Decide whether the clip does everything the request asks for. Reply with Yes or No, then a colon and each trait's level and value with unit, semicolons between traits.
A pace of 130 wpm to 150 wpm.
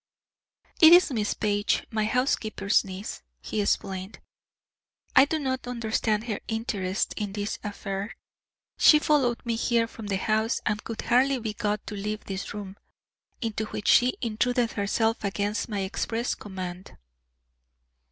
Yes: average, 140 wpm